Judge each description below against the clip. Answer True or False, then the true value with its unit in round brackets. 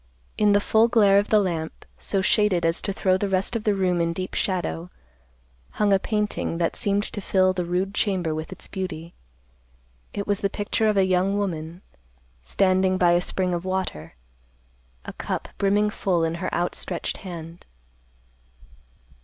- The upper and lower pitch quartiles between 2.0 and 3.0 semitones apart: True (2.7 semitones)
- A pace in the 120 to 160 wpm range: False (170 wpm)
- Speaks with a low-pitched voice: False (185 Hz)